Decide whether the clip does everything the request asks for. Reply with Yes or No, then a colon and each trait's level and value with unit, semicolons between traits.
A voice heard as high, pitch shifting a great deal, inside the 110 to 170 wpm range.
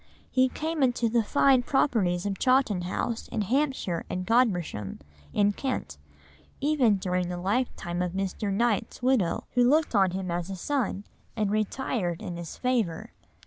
Yes: high, 210 Hz; wide, 5.8 semitones; average, 155 wpm